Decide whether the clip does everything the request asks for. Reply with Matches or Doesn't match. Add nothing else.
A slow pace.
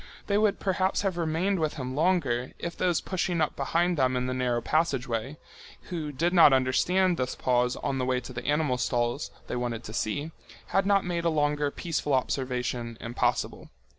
Doesn't match